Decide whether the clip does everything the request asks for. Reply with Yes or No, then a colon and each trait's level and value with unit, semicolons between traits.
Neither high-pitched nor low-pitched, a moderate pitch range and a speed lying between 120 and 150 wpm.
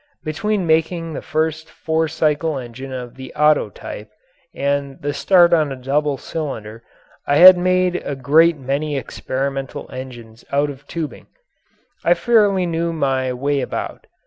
Yes: medium, 145 Hz; average, 3.4 semitones; average, 145 wpm